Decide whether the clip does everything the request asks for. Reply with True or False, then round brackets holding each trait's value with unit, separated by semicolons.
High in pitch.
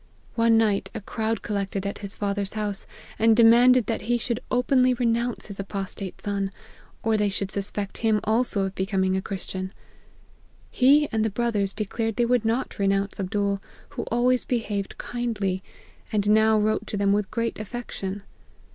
True (215 Hz)